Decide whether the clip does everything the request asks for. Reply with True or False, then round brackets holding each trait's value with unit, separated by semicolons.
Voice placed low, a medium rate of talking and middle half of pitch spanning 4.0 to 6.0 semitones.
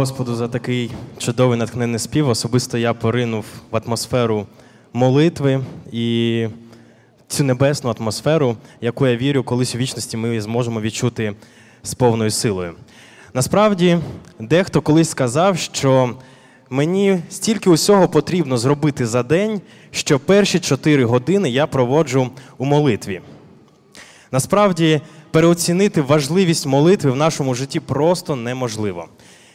True (130 Hz; 115 wpm; 4.9 semitones)